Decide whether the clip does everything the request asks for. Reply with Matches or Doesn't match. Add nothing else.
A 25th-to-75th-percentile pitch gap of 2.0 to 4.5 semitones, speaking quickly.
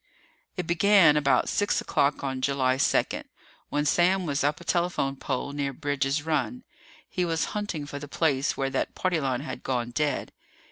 Doesn't match